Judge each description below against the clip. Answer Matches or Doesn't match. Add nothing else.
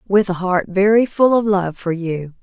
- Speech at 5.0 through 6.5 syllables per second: Doesn't match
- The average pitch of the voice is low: Doesn't match